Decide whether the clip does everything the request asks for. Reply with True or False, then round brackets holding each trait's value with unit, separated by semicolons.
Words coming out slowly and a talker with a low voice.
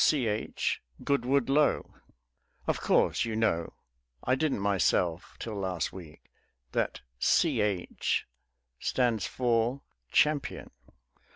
True (95 wpm; 115 Hz)